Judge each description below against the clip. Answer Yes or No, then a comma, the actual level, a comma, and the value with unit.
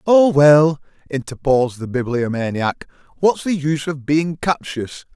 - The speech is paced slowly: Yes, slow, 130 wpm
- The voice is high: No, medium, 145 Hz